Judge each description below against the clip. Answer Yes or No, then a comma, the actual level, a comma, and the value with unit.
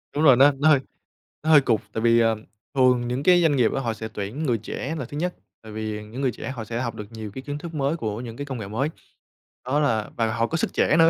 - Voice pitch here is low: Yes, low, 125 Hz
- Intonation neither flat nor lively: Yes, average, 4.4 semitones